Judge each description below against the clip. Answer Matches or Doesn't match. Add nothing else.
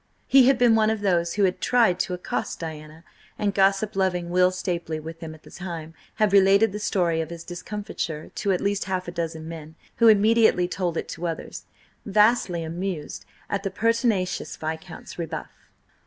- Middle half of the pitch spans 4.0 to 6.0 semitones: Doesn't match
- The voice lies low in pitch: Doesn't match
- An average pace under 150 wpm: Doesn't match